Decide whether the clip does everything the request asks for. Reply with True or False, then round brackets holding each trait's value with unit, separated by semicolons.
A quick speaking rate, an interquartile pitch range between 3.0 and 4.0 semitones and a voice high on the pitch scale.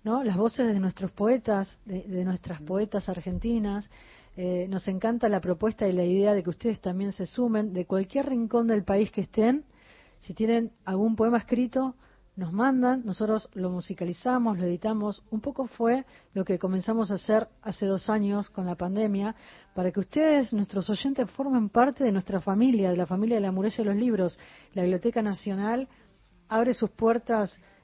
False (180 wpm; 3.3 semitones; 210 Hz)